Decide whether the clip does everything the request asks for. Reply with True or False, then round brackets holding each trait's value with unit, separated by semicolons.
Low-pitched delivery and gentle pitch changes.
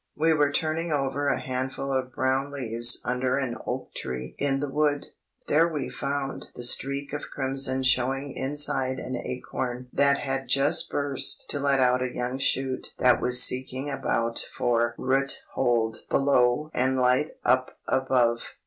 True (130 Hz; 1.8 semitones)